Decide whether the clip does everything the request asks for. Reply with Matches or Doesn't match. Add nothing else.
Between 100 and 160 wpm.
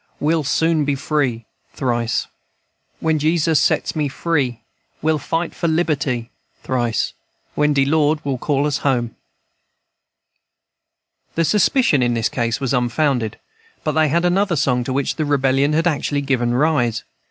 Matches